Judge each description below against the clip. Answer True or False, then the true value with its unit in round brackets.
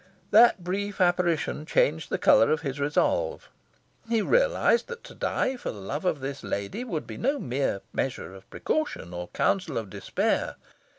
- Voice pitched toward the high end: False (165 Hz)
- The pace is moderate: True (165 wpm)